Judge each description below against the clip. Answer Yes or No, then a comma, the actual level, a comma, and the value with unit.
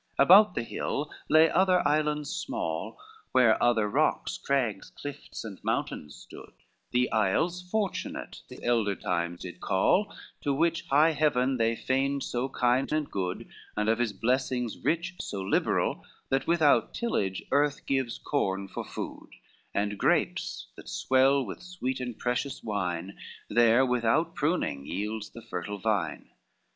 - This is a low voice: Yes, low, 125 Hz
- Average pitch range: No, wide, 5.8 semitones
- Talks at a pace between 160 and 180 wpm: No, average, 145 wpm